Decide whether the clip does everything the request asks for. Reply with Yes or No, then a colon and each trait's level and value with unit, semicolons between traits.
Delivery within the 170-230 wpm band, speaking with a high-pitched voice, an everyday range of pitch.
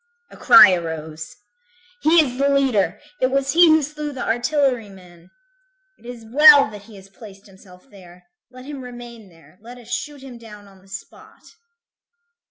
No: average, 175 wpm; high, 230 Hz; wide, 6.0 semitones